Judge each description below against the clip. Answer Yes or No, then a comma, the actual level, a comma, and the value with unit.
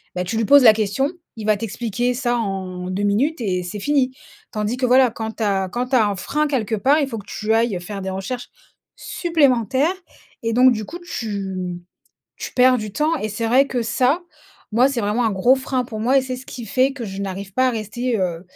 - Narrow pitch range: No, average, 4.1 semitones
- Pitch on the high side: Yes, high, 230 Hz